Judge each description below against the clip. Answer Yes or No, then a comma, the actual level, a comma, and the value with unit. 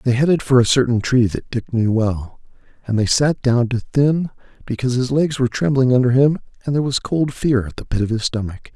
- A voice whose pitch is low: Yes, low, 125 Hz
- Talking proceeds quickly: Yes, fast, 235 wpm